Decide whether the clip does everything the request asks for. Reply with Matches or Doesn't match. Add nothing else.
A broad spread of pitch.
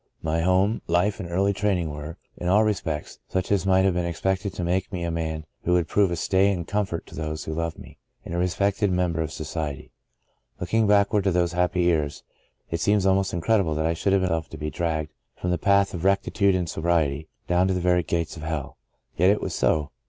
Doesn't match